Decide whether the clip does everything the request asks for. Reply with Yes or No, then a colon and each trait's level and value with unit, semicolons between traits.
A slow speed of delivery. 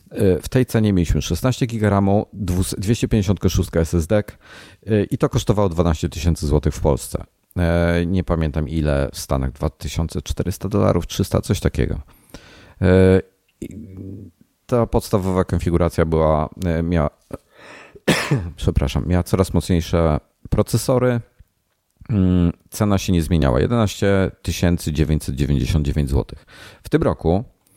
Yes: slow, 100 wpm